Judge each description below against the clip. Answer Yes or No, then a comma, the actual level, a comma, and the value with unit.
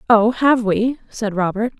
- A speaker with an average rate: Yes, average, 165 wpm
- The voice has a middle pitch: No, high, 225 Hz